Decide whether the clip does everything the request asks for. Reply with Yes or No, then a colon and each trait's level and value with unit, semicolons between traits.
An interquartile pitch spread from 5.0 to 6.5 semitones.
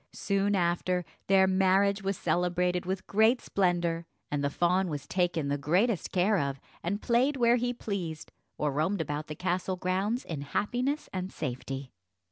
No: average, 3.5 semitones